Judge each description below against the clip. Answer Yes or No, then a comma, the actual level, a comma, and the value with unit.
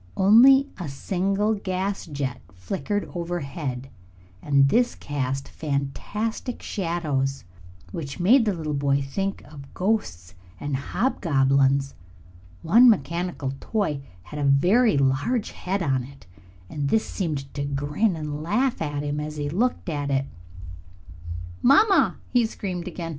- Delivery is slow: Yes, slow, 130 wpm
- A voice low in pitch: No, medium, 155 Hz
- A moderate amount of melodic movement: No, wide, 6.3 semitones